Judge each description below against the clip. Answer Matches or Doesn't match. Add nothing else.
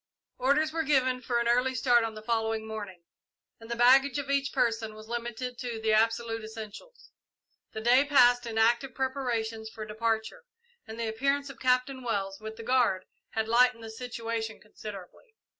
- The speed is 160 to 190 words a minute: Matches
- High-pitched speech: Matches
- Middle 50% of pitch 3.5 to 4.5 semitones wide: Doesn't match